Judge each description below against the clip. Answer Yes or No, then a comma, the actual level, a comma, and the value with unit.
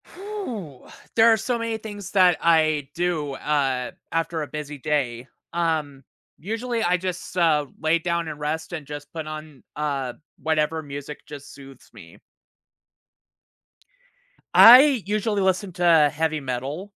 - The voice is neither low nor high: Yes, medium, 160 Hz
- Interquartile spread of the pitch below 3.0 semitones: No, average, 4.2 semitones